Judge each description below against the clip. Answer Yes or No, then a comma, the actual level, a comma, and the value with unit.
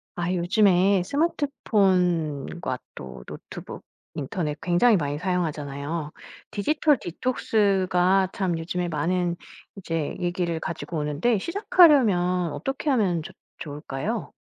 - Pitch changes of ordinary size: Yes, average, 4.0 semitones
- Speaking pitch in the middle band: Yes, medium, 180 Hz